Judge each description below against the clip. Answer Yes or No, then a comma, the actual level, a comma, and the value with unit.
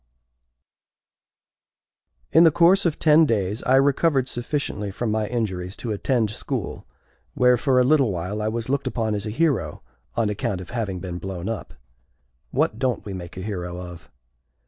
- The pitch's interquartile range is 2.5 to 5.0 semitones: No, wide, 5.5 semitones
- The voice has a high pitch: No, low, 110 Hz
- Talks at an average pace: Yes, average, 170 wpm